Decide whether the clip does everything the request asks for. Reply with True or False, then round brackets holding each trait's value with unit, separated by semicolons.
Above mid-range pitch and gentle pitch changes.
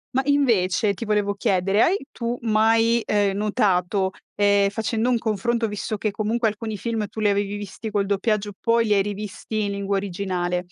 True (210 Hz; 2.2 semitones)